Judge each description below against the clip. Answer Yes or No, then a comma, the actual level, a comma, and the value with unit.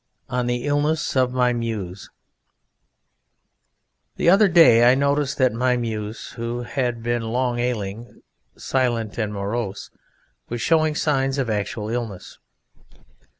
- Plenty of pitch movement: No, average, 2.8 semitones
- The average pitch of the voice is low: Yes, low, 120 Hz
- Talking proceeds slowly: Yes, slow, 125 wpm